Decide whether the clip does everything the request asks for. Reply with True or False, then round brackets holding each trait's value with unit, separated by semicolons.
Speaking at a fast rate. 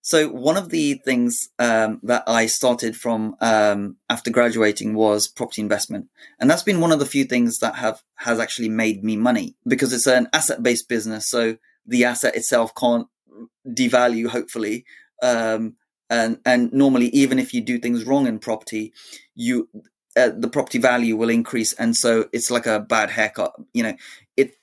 False (175 wpm)